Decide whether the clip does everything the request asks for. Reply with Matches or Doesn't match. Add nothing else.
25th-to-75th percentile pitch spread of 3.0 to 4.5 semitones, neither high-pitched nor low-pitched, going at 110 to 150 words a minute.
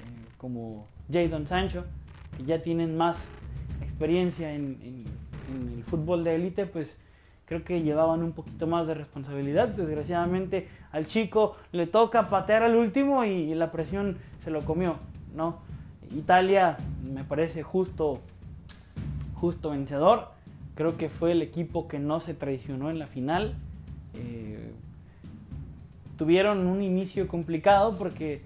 Doesn't match